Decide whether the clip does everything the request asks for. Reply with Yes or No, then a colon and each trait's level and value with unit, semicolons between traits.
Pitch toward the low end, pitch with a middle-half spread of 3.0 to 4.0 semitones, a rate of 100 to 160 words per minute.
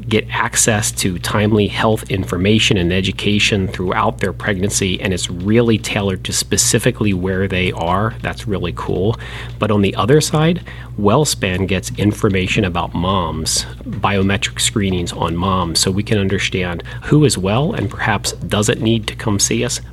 Yes: low, 105 Hz; average, 3.6 semitones; average, 155 wpm